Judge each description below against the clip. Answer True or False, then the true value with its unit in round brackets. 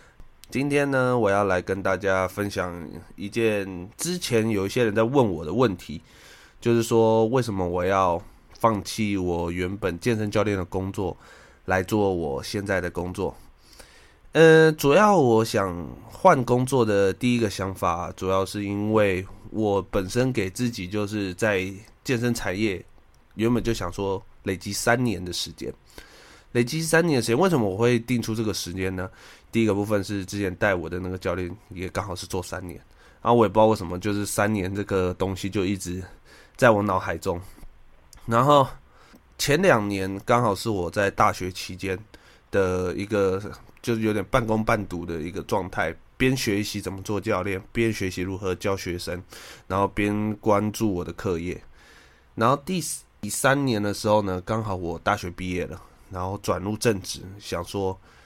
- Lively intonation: False (3.4 semitones)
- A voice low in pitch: True (100 Hz)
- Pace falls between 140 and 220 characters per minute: False (250 characters per minute)